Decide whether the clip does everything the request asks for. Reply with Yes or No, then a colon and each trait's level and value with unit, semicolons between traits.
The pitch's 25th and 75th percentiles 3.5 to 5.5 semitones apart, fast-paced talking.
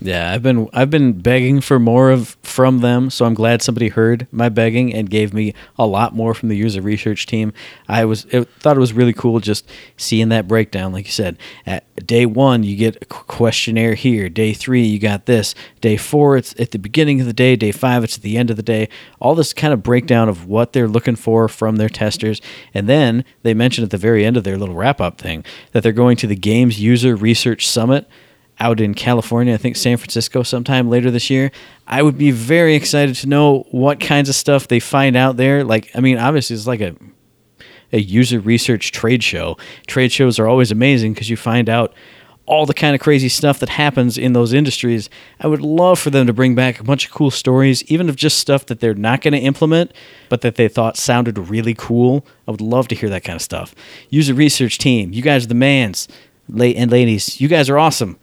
No: average, 3.0 semitones; fast, 230 wpm